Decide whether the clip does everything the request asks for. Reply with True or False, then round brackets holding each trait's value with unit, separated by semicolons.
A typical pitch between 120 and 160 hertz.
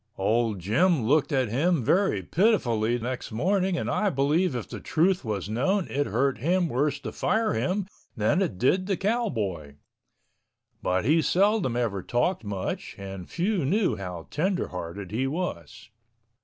True (135 Hz)